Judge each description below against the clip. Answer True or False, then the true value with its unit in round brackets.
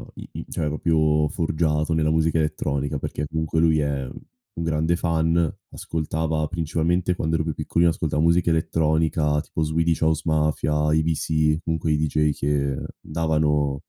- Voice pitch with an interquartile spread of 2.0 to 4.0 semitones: False (1.2 semitones)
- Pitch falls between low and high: False (80 Hz)